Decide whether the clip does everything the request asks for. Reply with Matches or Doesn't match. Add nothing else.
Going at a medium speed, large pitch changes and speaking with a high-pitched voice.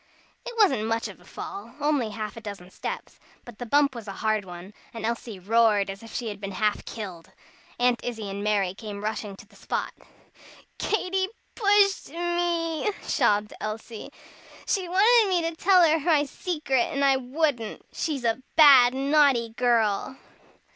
Matches